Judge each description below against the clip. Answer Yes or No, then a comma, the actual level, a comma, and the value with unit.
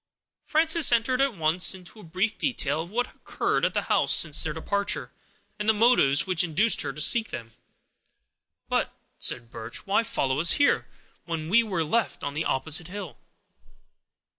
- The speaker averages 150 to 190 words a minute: Yes, average, 175 wpm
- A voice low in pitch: No, medium, 185 Hz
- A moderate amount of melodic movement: No, wide, 6.7 semitones